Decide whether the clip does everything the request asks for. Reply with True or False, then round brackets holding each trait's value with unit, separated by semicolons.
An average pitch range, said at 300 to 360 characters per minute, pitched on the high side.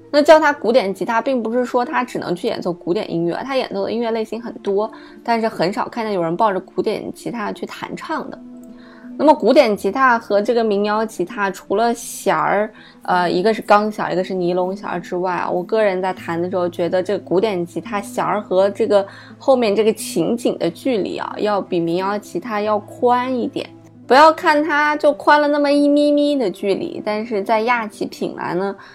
True (4.6 semitones; 305 characters per minute; 220 Hz)